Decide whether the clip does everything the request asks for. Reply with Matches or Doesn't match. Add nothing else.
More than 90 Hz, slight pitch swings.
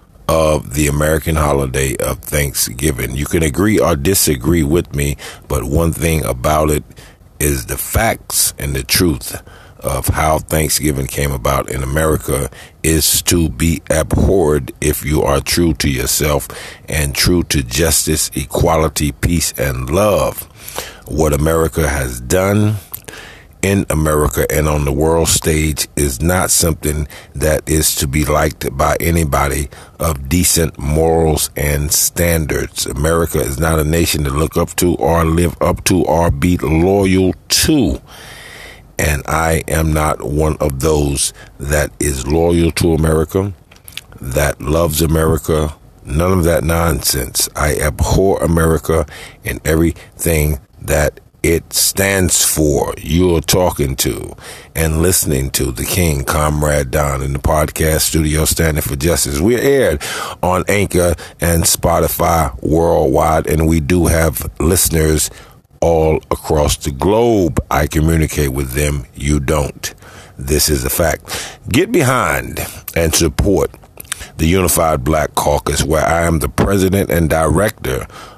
Doesn't match